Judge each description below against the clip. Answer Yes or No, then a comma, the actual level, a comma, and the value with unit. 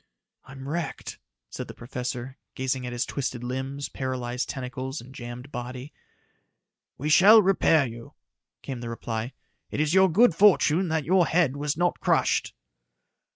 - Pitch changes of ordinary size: Yes, average, 4.3 semitones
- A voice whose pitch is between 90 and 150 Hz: Yes, low, 135 Hz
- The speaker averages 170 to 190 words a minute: No, average, 150 wpm